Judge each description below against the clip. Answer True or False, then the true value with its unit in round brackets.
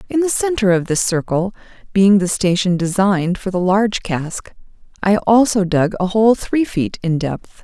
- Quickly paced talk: False (180 wpm)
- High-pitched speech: True (195 Hz)